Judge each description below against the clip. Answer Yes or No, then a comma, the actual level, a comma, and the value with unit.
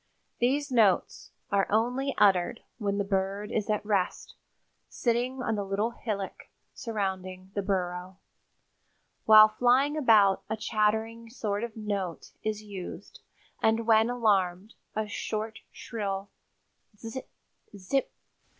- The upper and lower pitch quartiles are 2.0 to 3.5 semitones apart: Yes, average, 2.7 semitones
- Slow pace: Yes, slow, 120 wpm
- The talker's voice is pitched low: No, high, 215 Hz